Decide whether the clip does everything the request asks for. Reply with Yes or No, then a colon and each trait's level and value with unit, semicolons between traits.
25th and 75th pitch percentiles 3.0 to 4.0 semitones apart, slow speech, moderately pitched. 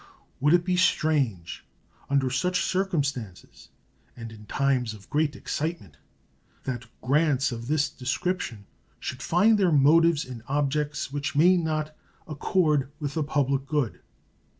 Yes: average, 3.7 semitones; slow, 130 wpm; medium, 145 Hz